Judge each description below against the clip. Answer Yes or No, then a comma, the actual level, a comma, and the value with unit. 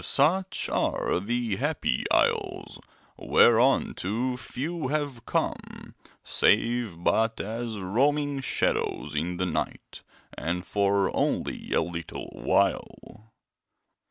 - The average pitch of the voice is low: Yes, low, 115 Hz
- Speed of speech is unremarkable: No, slow, 100 wpm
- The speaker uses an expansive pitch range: Yes, wide, 5.8 semitones